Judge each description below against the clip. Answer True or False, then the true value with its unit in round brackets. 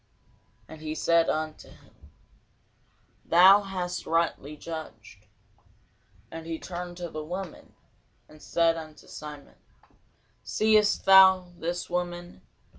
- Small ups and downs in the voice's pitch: True (2.3 semitones)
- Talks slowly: True (110 wpm)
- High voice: False (170 Hz)